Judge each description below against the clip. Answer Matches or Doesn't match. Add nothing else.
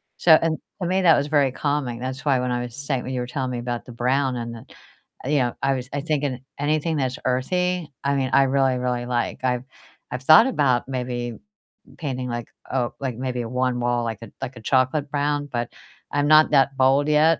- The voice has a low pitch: Matches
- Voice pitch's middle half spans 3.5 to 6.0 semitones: Doesn't match